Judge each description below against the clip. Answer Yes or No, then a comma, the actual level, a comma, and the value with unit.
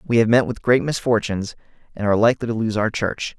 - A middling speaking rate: No, fast, 230 wpm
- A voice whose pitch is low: Yes, low, 115 Hz